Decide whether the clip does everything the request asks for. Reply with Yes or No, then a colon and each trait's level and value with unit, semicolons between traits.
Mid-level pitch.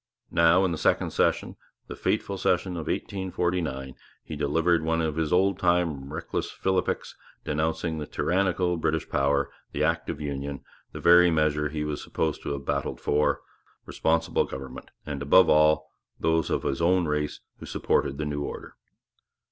No: very low, 80 Hz